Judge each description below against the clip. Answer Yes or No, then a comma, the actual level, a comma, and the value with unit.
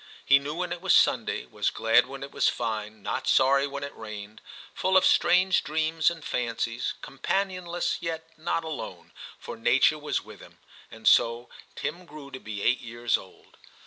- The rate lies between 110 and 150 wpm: No, average, 175 wpm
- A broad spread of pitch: Yes, wide, 6.2 semitones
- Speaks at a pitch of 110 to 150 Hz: Yes, medium, 140 Hz